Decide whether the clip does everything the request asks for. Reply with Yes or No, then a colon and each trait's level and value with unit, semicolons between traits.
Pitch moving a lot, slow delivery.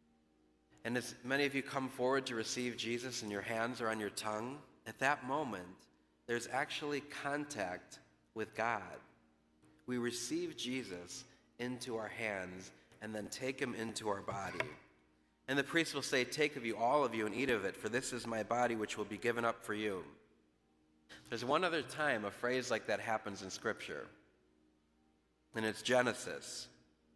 No: wide, 8.2 semitones; average, 175 wpm